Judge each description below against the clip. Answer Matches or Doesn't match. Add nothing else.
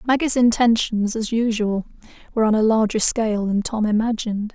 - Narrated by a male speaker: Doesn't match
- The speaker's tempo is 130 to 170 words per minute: Matches